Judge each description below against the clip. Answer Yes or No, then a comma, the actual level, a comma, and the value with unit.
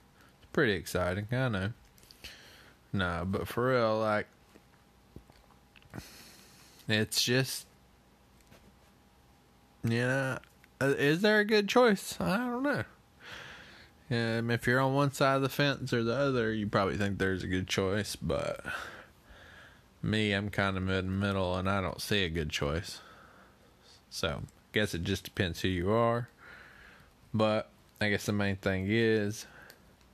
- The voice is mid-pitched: No, low, 105 Hz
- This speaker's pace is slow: No, average, 145 wpm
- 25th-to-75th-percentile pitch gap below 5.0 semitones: No, wide, 5.4 semitones